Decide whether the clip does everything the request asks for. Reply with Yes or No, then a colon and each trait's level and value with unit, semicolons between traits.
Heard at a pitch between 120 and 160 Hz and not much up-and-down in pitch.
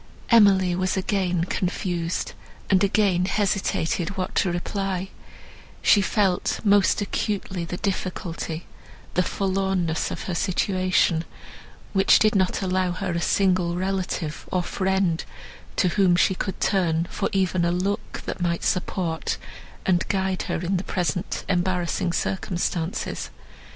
No: medium, 185 Hz; narrow, 1.8 semitones